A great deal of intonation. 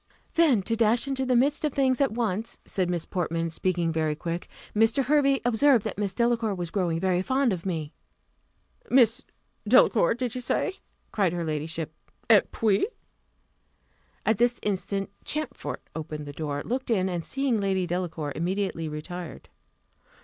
Yes: wide, 6.2 semitones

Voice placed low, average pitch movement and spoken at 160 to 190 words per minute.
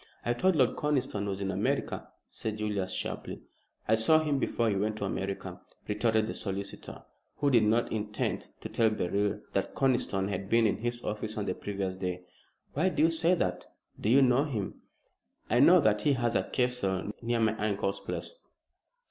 Yes: low, 110 Hz; average, 3.8 semitones; average, 185 wpm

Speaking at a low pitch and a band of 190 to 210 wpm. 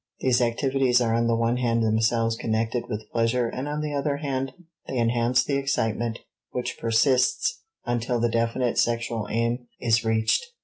No: low, 120 Hz; average, 165 wpm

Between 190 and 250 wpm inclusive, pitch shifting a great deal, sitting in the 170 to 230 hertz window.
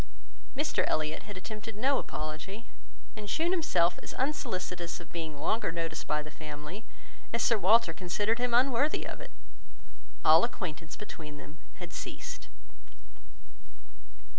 No: slow, 135 wpm; wide, 6.4 semitones; medium, 185 Hz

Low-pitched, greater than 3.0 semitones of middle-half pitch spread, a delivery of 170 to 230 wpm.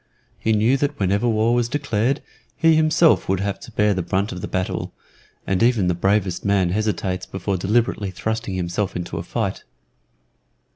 Yes: low, 105 Hz; average, 3.9 semitones; average, 175 wpm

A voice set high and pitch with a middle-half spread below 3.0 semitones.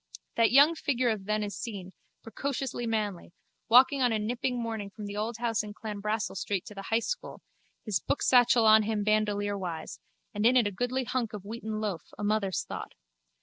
Yes: high, 215 Hz; narrow, 2.6 semitones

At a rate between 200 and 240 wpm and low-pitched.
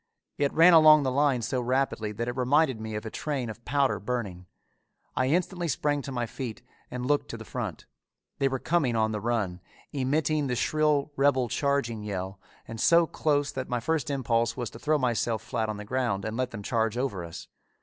Yes: fast, 205 wpm; low, 125 Hz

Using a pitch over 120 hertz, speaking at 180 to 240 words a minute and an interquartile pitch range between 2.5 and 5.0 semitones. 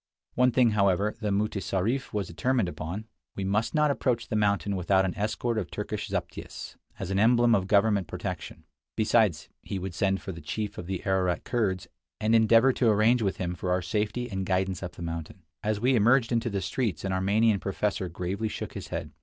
No: low, 100 Hz; average, 200 wpm; average, 3.2 semitones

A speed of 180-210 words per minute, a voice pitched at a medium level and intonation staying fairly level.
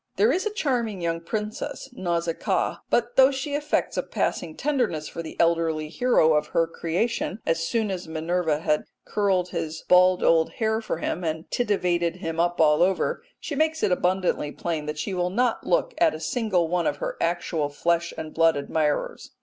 No: average, 185 wpm; medium, 175 Hz; average, 5.1 semitones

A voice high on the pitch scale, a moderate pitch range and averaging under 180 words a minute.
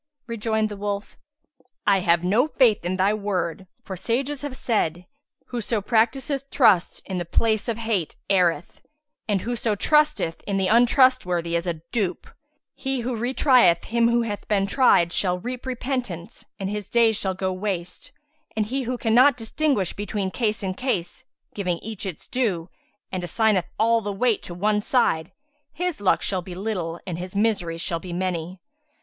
Yes: high, 205 Hz; average, 4.6 semitones; average, 170 wpm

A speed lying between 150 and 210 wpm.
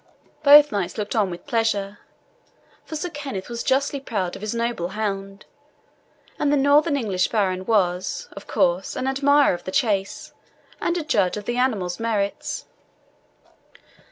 Yes: average, 155 wpm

